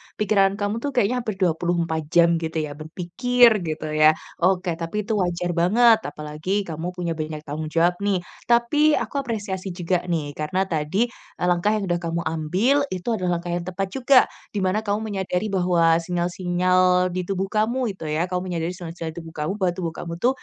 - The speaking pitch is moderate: Yes, medium, 180 Hz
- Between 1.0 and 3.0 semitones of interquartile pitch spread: No, average, 3.4 semitones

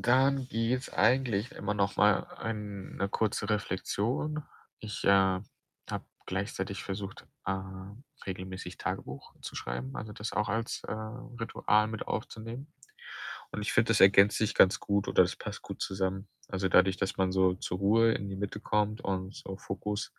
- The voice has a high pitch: No, low, 100 Hz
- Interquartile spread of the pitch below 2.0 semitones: No, narrow, 2.6 semitones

